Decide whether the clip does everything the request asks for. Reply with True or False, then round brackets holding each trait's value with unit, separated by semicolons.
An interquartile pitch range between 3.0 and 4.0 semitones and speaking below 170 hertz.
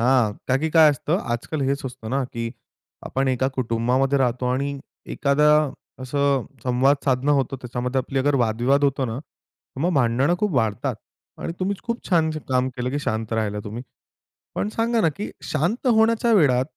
True (3.5 semitones; 135 Hz)